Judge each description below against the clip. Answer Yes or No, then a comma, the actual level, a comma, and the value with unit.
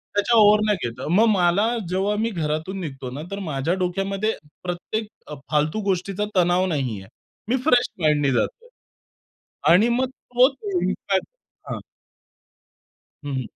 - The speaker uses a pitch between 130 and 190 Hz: Yes, medium, 185 Hz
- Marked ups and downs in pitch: Yes, wide, 5.7 semitones